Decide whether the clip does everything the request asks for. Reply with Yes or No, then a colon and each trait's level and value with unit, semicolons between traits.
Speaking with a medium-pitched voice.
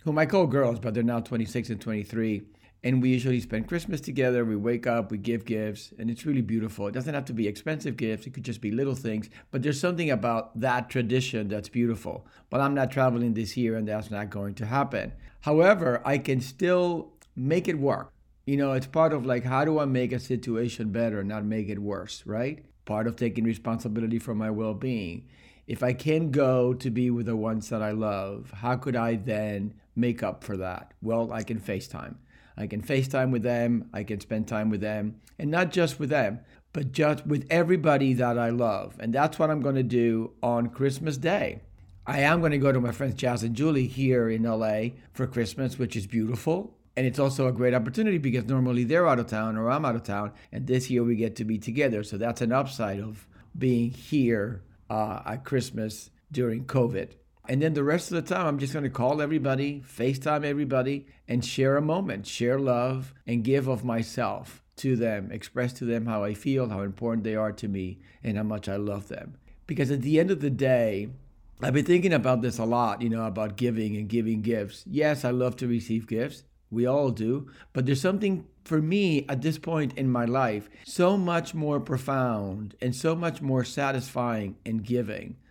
No: low, 125 Hz